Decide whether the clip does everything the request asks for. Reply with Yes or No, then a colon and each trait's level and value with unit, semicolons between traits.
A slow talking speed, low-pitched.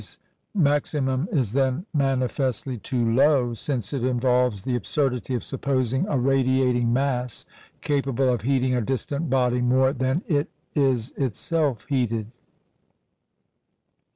Yes: slow, 125 wpm; low, 130 Hz